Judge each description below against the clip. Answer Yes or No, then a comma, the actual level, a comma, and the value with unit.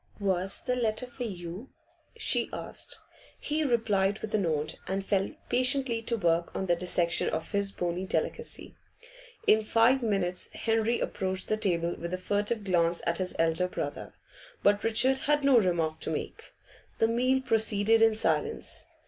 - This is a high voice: Yes, high, 205 Hz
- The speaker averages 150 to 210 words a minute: Yes, average, 160 wpm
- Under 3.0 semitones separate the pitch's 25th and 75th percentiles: No, average, 4.2 semitones